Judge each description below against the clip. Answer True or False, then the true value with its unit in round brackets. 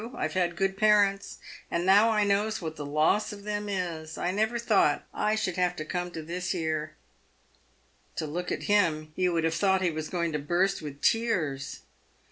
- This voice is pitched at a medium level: True (180 Hz)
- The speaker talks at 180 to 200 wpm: True (190 wpm)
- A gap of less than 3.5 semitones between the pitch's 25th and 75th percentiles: False (4.2 semitones)